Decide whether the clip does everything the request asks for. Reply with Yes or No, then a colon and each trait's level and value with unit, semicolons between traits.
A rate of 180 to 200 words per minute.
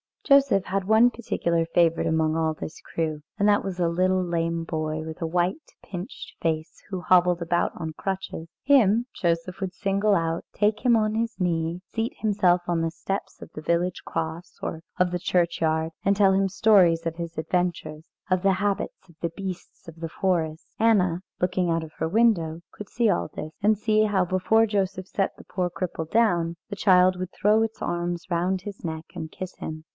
Yes: average, 195 wpm